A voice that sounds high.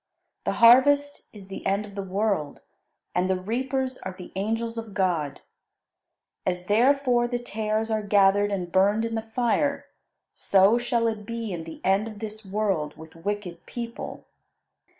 Yes: high, 210 Hz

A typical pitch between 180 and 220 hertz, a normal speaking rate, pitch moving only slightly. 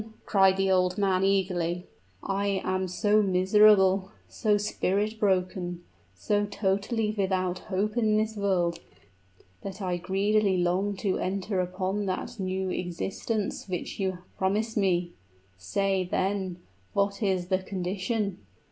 No: high, 190 Hz; slow, 125 wpm; narrow, 1.8 semitones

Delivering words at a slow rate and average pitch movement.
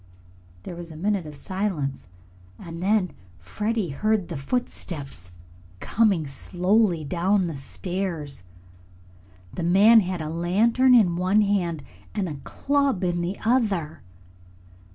Yes: slow, 125 wpm; average, 4.5 semitones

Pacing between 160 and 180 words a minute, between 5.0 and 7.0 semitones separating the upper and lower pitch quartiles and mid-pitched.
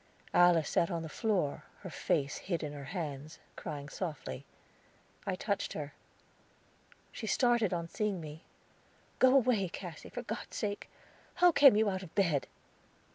No: average, 150 wpm; wide, 5.6 semitones; medium, 180 Hz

